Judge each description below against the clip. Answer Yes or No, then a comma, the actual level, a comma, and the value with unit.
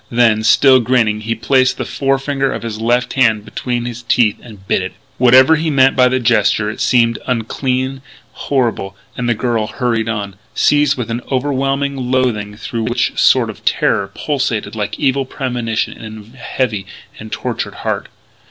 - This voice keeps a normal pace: Yes, average, 170 wpm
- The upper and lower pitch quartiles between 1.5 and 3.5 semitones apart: Yes, average, 2.9 semitones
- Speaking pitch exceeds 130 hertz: No, low, 120 Hz